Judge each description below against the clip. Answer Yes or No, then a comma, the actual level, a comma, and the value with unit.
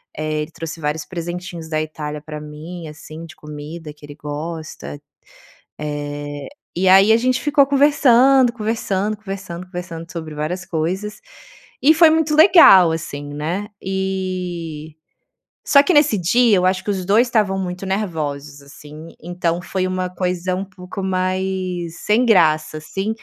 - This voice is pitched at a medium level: Yes, medium, 180 Hz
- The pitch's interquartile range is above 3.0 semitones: Yes, average, 4.1 semitones